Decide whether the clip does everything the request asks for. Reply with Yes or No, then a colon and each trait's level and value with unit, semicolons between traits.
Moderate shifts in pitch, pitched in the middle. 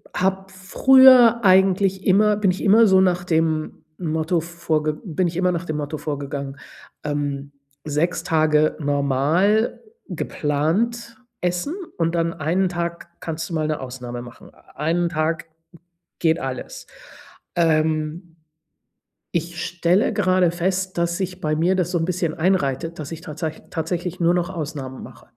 Yes: average, 3.2 semitones; medium, 170 Hz